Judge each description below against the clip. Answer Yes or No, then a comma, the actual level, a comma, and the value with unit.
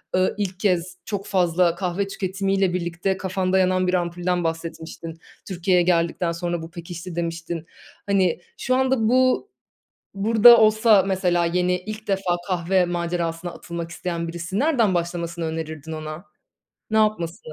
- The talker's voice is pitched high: No, medium, 180 Hz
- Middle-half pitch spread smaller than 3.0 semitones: Yes, narrow, 2.4 semitones